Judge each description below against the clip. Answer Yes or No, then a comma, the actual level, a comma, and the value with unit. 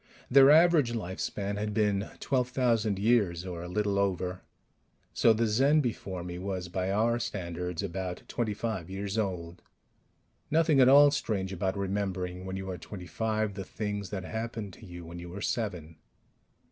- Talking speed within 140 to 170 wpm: Yes, average, 165 wpm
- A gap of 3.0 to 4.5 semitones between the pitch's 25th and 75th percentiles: Yes, average, 3.7 semitones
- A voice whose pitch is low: Yes, low, 100 Hz